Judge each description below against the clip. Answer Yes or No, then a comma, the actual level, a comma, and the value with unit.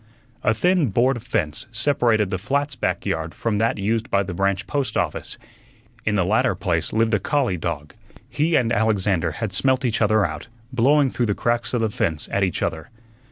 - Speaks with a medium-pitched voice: No, low, 110 Hz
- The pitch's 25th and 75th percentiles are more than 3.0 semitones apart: Yes, average, 4.6 semitones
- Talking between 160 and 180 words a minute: No, average, 195 wpm